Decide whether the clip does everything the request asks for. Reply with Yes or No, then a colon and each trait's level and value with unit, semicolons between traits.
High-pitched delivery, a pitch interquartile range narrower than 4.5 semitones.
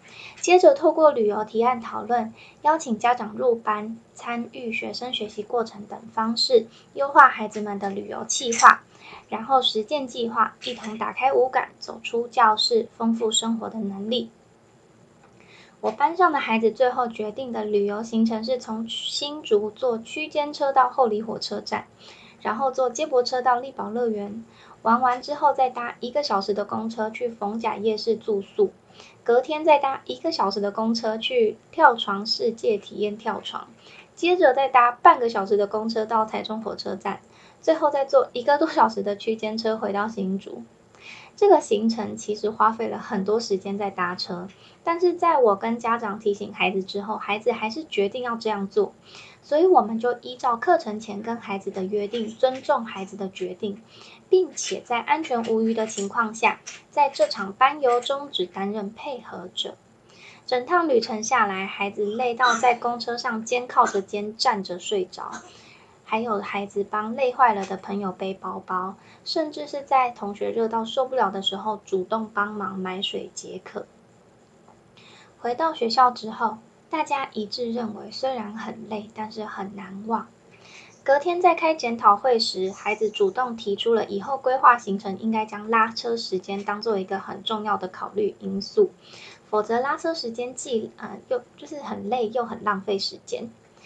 Yes: high, 225 Hz; average, 3.8 semitones